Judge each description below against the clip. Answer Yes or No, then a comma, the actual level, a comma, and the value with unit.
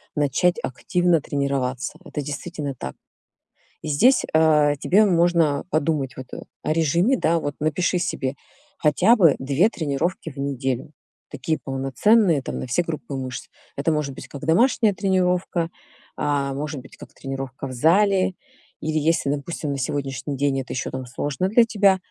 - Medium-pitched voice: Yes, medium, 150 Hz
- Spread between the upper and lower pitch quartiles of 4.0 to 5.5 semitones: Yes, average, 4.3 semitones